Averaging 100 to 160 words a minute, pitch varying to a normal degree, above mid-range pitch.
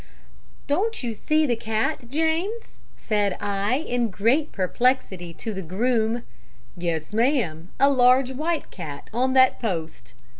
No: slow, 135 wpm; wide, 5.7 semitones; high, 235 Hz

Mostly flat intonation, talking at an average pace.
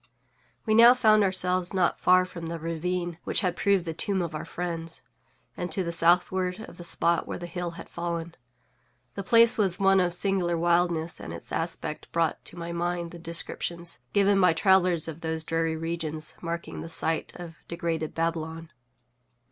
Yes: narrow, 1.8 semitones; average, 180 wpm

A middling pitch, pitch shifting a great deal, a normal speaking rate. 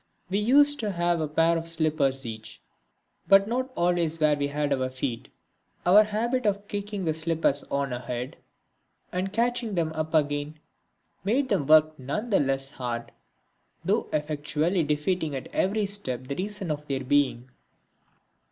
Yes: medium, 160 Hz; wide, 5.9 semitones; average, 155 wpm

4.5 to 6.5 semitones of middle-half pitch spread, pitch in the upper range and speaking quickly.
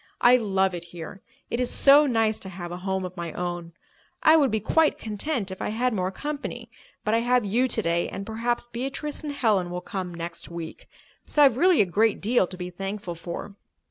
Yes: wide, 5.5 semitones; high, 205 Hz; fast, 210 wpm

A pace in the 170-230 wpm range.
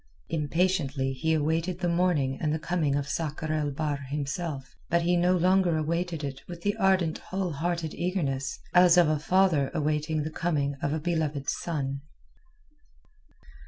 No: average, 160 wpm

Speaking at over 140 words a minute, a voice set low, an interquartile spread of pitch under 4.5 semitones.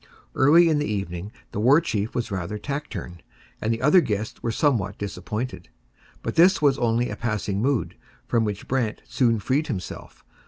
No: average, 170 wpm; low, 115 Hz; average, 5.0 semitones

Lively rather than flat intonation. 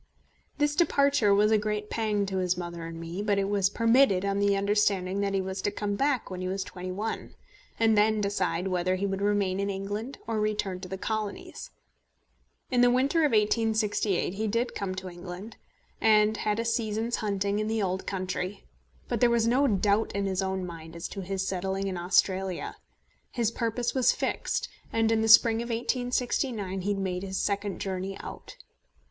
No: average, 2.8 semitones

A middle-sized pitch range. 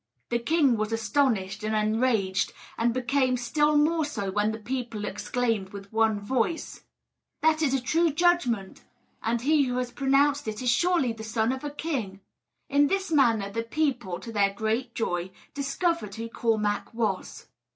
Yes: average, 4.8 semitones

